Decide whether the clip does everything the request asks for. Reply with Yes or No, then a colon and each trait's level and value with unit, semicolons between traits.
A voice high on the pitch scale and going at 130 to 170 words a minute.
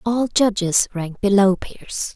Yes: high, 205 Hz; average, 140 wpm